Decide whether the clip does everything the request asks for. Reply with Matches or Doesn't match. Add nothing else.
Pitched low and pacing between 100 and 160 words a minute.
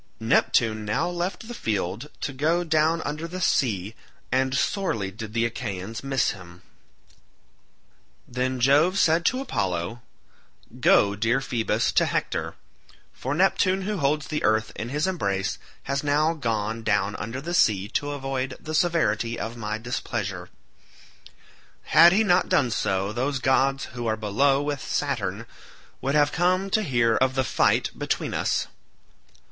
Matches